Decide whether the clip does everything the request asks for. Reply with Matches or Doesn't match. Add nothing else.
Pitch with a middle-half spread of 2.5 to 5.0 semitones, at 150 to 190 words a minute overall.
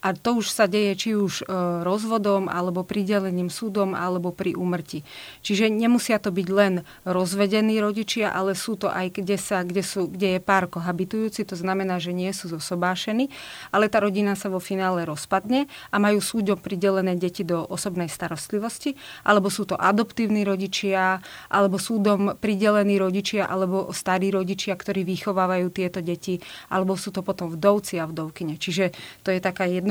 Doesn't match